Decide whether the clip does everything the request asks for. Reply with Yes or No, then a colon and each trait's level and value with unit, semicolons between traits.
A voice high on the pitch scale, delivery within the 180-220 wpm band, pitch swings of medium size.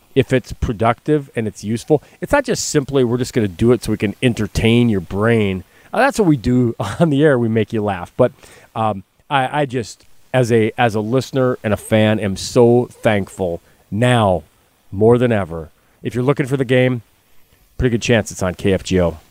No: low, 115 Hz; average, 200 wpm; average, 4.1 semitones